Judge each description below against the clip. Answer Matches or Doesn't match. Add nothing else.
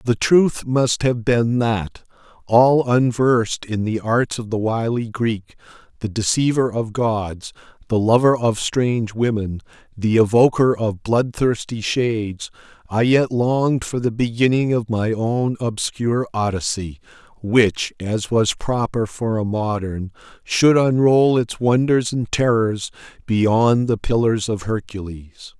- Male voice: Matches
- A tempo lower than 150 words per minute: Matches